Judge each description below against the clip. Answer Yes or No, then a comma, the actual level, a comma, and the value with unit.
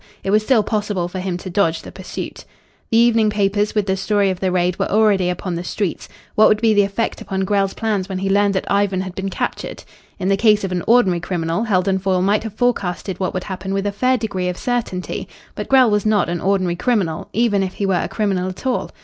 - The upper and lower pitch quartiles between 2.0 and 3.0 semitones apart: Yes, narrow, 2.4 semitones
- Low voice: No, high, 195 Hz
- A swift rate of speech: Yes, fast, 240 wpm